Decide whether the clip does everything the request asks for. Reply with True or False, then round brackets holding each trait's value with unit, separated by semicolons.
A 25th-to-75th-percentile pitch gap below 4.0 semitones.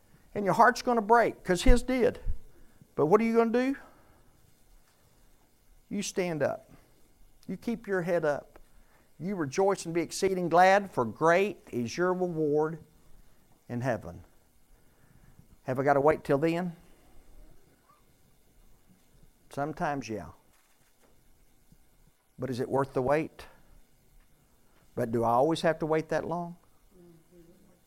False (5.1 semitones)